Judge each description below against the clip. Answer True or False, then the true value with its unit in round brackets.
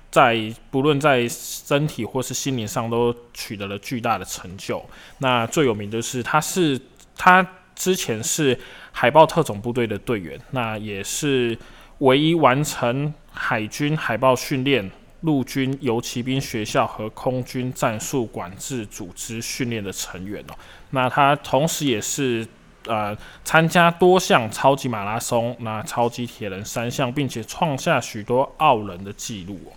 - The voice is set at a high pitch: False (125 Hz)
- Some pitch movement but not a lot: True (3.9 semitones)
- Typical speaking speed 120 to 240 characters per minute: True (225 characters per minute)